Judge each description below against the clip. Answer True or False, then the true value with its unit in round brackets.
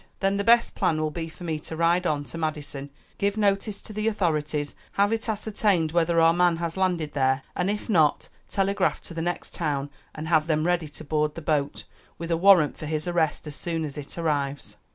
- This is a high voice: False (165 Hz)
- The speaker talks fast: True (215 wpm)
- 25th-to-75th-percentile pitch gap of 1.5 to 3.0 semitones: False (3.6 semitones)